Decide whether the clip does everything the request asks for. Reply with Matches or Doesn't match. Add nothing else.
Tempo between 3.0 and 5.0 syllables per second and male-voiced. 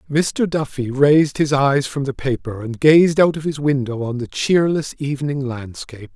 Matches